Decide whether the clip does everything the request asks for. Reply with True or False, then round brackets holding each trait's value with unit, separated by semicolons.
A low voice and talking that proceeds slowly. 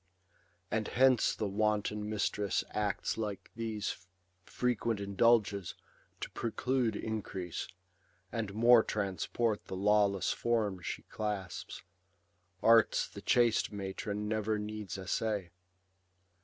True (105 Hz; 100 wpm)